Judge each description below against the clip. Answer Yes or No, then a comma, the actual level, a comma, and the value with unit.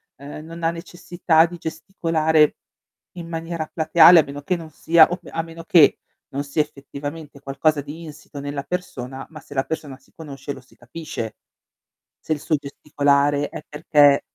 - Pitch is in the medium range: Yes, medium, 155 Hz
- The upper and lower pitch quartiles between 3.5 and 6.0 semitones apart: No, narrow, 2.6 semitones